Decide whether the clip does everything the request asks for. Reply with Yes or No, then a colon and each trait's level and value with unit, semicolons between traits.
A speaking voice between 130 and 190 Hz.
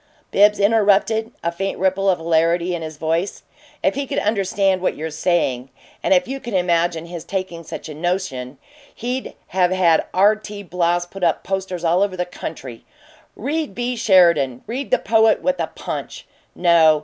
Yes: medium, 185 Hz